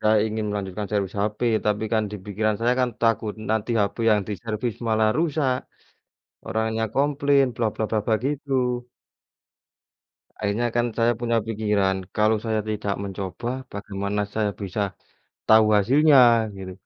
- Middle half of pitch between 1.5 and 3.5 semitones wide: Yes, narrow, 2.5 semitones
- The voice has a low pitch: Yes, low, 110 Hz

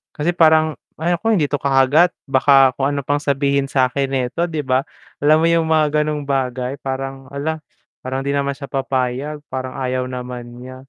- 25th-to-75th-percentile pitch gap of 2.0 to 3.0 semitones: Yes, narrow, 2.6 semitones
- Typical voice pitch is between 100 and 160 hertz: Yes, medium, 140 Hz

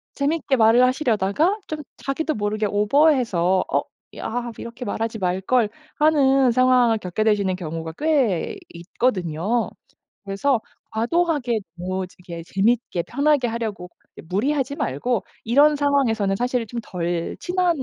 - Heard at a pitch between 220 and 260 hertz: Yes, high, 230 Hz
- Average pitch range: No, wide, 6.1 semitones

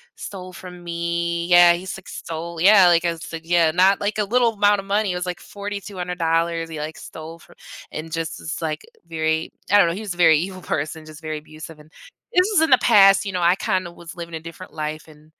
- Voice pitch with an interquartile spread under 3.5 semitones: Yes, average, 2.9 semitones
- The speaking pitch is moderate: Yes, medium, 170 Hz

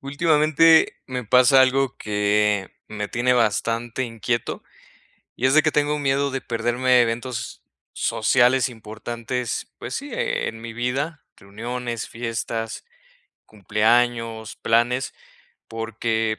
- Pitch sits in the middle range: No, low, 120 Hz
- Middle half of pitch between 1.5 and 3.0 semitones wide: Yes, average, 2.7 semitones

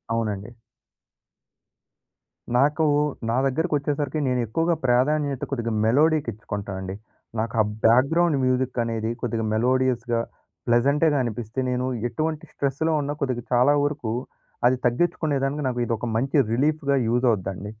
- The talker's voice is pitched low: Yes, low, 130 Hz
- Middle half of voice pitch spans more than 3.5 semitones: Yes, average, 3.9 semitones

